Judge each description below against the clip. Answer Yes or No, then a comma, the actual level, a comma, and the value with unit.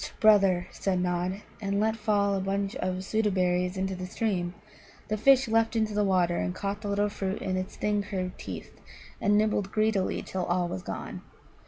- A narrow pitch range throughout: Yes, narrow, 2.3 semitones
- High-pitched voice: Yes, high, 195 Hz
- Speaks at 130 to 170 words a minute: No, average, 195 wpm